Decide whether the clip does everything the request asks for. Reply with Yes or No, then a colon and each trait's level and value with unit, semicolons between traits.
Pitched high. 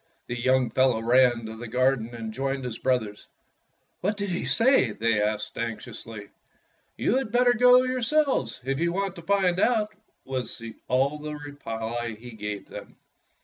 No: low, 130 Hz